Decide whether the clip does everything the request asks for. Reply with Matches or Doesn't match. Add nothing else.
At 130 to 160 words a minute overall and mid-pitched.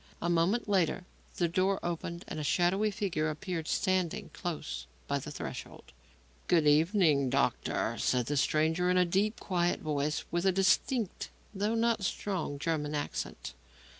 Matches